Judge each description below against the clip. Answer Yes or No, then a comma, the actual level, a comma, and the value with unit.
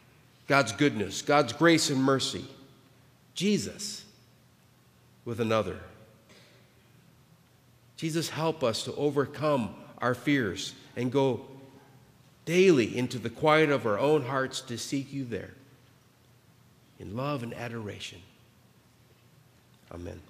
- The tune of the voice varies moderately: Yes, average, 3.6 semitones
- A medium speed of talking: No, slow, 105 wpm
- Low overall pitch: Yes, low, 130 Hz